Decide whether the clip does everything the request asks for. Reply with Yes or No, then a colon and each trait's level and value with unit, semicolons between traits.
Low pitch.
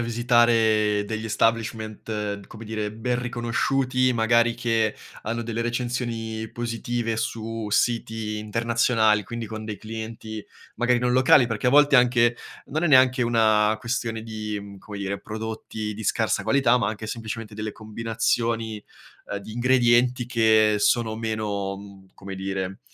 Yes: low, 115 Hz